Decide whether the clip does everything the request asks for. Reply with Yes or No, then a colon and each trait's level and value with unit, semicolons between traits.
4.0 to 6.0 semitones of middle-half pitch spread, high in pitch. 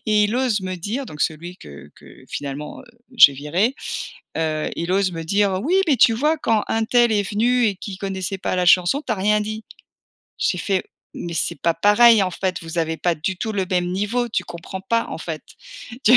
Yes: average, 4.3 semitones; high, 195 Hz